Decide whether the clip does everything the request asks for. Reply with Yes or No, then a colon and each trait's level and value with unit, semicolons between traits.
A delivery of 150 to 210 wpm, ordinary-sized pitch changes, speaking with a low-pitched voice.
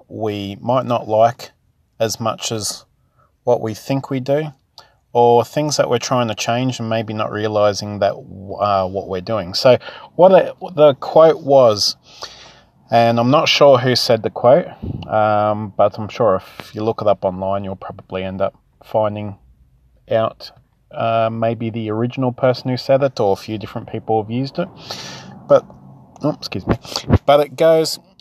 Yes: average, 170 wpm; average, 4.1 semitones; low, 115 Hz